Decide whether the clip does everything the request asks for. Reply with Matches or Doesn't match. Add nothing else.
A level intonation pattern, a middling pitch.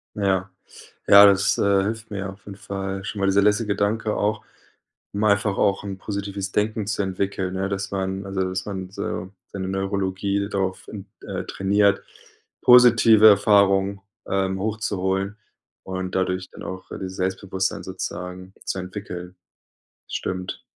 Doesn't match